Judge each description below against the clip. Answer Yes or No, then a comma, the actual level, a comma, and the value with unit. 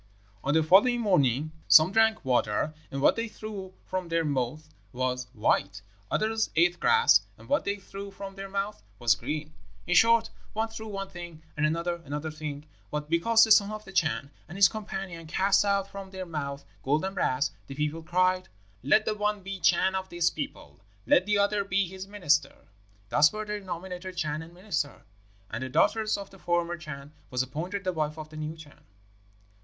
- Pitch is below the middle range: No, medium, 175 Hz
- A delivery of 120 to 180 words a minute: No, average, 190 wpm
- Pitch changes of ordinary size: Yes, average, 4.6 semitones